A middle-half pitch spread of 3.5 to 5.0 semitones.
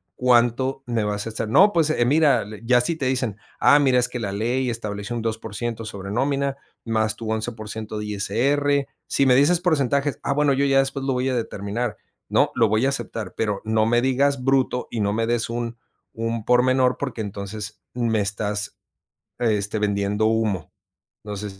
Yes: average, 3.8 semitones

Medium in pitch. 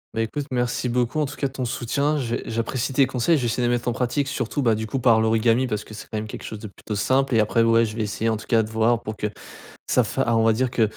No: low, 115 Hz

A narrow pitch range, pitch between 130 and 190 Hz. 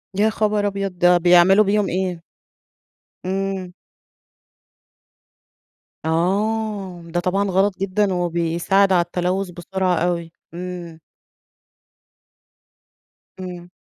Yes: narrow, 2.1 semitones; medium, 185 Hz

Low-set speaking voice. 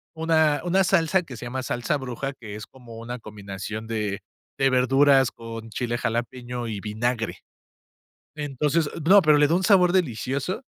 Yes: low, 125 Hz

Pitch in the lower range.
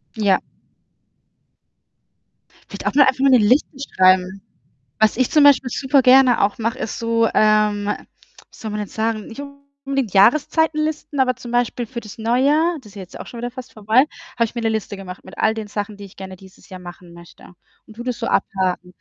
No: high, 225 Hz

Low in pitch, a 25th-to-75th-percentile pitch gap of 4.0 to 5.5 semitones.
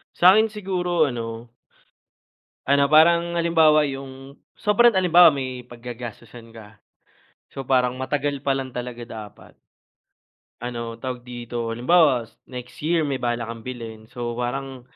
Yes: low, 130 Hz; average, 4.3 semitones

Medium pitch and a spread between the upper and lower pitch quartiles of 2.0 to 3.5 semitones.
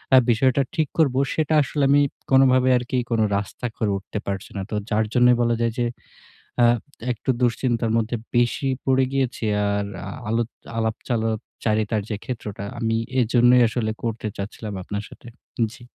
No: low, 120 Hz; narrow, 2.6 semitones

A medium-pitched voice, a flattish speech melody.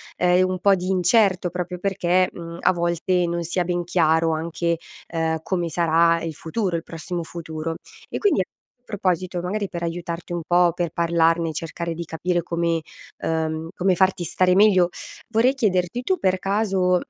Yes: medium, 175 Hz; narrow, 1.7 semitones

